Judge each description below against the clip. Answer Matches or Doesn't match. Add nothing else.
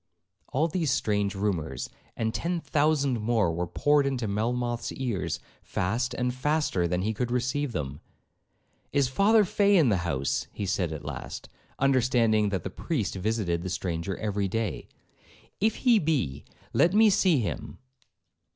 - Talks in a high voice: Doesn't match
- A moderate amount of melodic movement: Doesn't match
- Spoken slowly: Doesn't match